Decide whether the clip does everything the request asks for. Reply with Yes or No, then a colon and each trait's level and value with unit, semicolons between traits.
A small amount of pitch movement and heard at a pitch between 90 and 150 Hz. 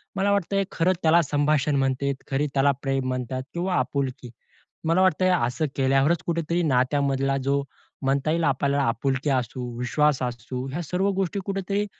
No: average, 4.2 semitones; medium, 140 Hz